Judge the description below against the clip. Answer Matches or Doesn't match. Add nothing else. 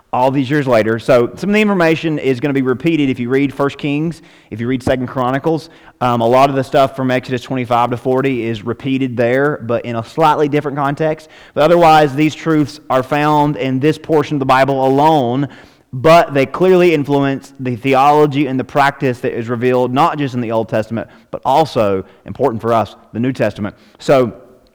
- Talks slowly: Doesn't match